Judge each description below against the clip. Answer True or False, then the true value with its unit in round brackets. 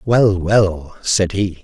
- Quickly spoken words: False (145 wpm)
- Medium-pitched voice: False (95 Hz)